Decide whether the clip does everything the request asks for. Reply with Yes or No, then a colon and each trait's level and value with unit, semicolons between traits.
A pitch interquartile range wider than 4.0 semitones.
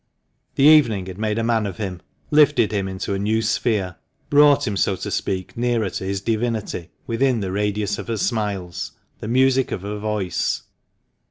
No: average, 3.2 semitones